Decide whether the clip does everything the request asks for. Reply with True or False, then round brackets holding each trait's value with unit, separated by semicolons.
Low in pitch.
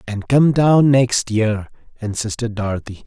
True (115 Hz)